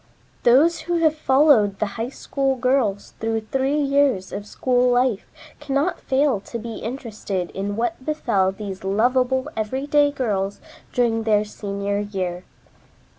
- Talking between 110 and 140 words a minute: Yes, slow, 135 wpm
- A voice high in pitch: Yes, high, 235 Hz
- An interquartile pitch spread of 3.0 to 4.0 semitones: No, average, 4.9 semitones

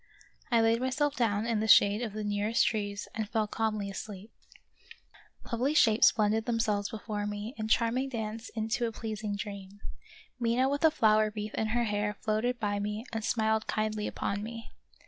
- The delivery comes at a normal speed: Yes, average, 175 wpm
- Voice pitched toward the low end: No, high, 220 Hz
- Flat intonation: Yes, narrow, 1.8 semitones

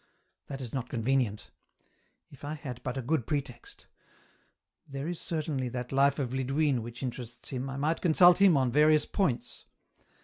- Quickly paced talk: No, average, 165 wpm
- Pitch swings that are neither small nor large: Yes, average, 3.5 semitones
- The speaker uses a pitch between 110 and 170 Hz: Yes, low, 135 Hz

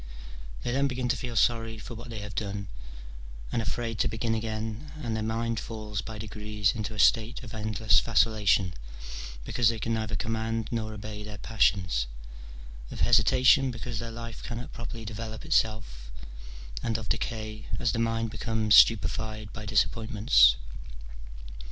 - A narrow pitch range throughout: Yes, narrow, 1.4 semitones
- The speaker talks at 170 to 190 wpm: No, average, 155 wpm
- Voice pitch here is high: No, low, 110 Hz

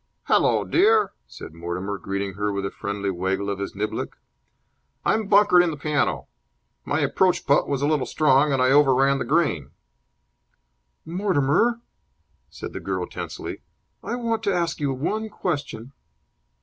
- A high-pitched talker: No, medium, 140 Hz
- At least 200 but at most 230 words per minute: No, average, 155 wpm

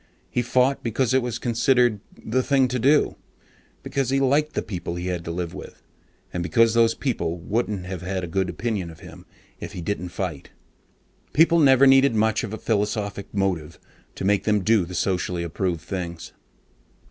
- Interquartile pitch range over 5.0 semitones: Yes, wide, 5.6 semitones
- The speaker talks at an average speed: Yes, average, 180 wpm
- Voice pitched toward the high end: No, low, 105 Hz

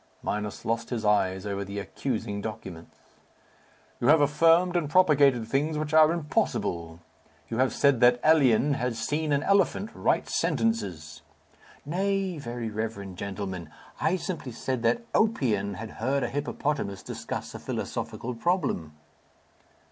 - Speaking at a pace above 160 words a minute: No, slow, 135 wpm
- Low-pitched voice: Yes, low, 125 Hz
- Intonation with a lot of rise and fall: Yes, wide, 6.7 semitones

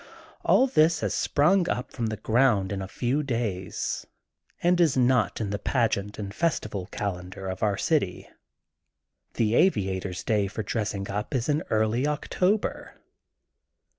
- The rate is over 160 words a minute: No, average, 150 wpm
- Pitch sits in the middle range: No, low, 110 Hz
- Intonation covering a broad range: Yes, wide, 6.2 semitones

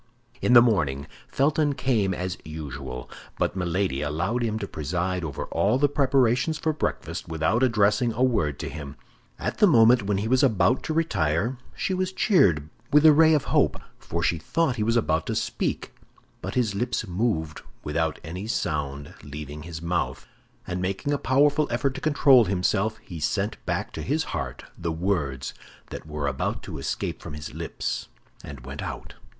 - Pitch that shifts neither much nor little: No, wide, 8.5 semitones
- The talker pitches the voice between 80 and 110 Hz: Yes, low, 100 Hz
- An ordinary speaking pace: Yes, average, 180 wpm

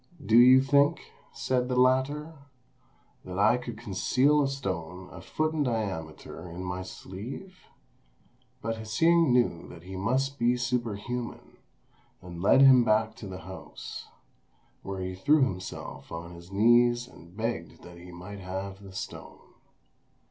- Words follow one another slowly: No, average, 145 wpm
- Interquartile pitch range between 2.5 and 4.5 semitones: No, wide, 5.5 semitones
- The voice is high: No, low, 110 Hz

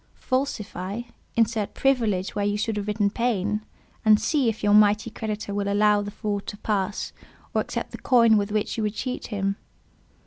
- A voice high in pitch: Yes, high, 210 Hz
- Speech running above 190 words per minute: No, average, 180 wpm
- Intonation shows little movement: Yes, narrow, 1.8 semitones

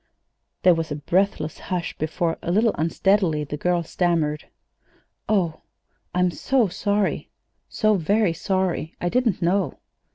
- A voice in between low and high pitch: Yes, medium, 180 Hz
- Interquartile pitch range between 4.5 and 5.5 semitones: No, average, 3.5 semitones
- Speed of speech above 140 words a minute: No, slow, 135 wpm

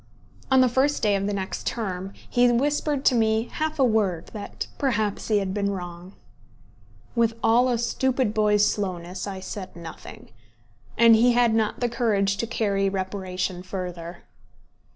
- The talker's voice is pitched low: No, high, 210 Hz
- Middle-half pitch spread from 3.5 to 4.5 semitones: Yes, average, 3.9 semitones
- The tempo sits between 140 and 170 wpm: Yes, average, 160 wpm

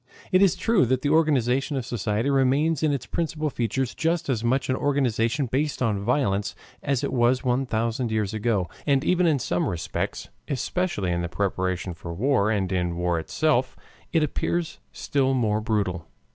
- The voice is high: No, low, 125 Hz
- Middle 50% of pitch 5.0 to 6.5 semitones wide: Yes, wide, 5.6 semitones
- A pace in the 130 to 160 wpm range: No, average, 175 wpm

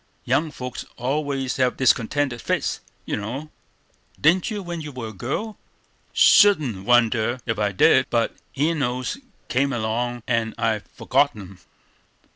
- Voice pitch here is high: No, low, 125 Hz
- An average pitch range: Yes, average, 4.3 semitones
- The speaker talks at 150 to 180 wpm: No, slow, 135 wpm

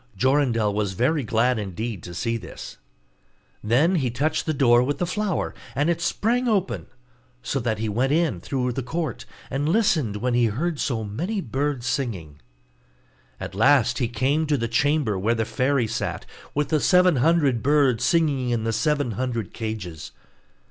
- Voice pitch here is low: Yes, low, 130 Hz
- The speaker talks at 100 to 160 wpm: No, average, 170 wpm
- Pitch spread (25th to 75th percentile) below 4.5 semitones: No, average, 4.9 semitones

